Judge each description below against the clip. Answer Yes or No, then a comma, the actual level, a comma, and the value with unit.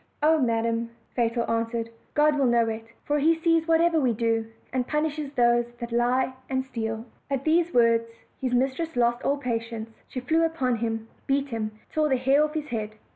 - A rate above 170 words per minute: Yes, average, 190 wpm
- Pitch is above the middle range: Yes, very high, 250 Hz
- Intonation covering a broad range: No, average, 4.4 semitones